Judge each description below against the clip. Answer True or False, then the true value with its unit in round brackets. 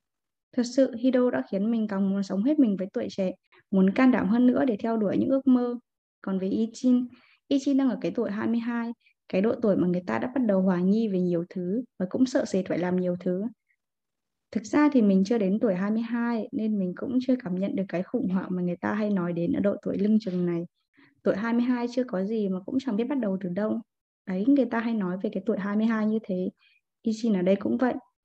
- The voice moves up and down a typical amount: True (4.5 semitones)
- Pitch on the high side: True (220 Hz)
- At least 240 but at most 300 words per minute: True (245 wpm)